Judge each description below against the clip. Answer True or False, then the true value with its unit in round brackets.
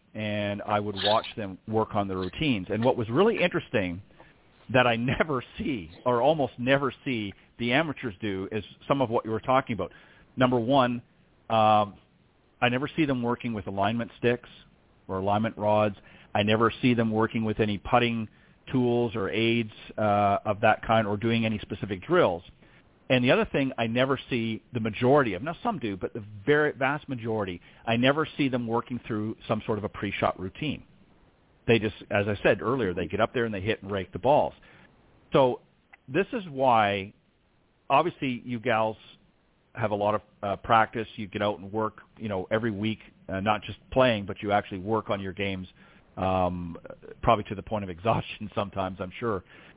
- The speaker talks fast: False (190 wpm)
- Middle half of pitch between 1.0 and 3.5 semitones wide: True (3.2 semitones)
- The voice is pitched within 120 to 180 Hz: False (110 Hz)